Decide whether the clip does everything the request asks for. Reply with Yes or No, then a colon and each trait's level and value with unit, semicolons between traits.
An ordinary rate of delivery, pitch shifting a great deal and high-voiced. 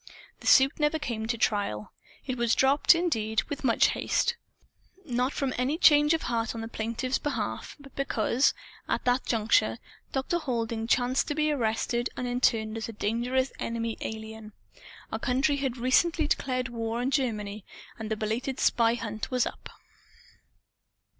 No: average, 160 wpm; average, 3.2 semitones; high, 245 Hz